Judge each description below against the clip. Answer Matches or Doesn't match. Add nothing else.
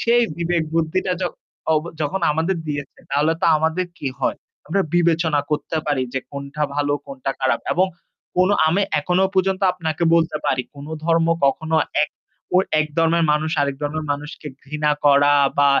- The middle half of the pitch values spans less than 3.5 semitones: Matches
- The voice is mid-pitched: Matches